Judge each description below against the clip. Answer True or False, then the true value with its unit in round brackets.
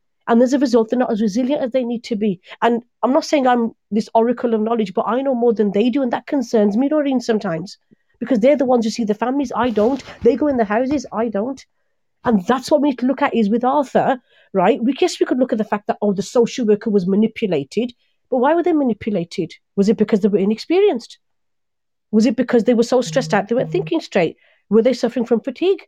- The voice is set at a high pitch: True (240 Hz)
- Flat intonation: False (3.2 semitones)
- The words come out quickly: True (245 wpm)